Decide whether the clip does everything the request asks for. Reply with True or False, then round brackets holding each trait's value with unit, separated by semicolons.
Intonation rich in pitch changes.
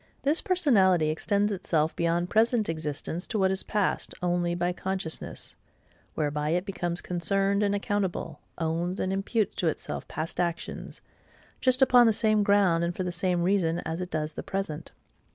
False (3.3 semitones)